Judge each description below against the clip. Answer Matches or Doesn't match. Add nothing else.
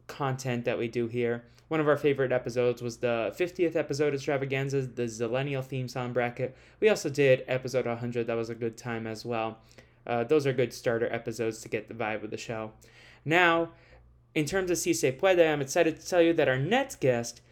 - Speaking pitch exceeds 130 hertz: Doesn't match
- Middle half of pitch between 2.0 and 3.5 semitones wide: Doesn't match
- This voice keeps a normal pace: Doesn't match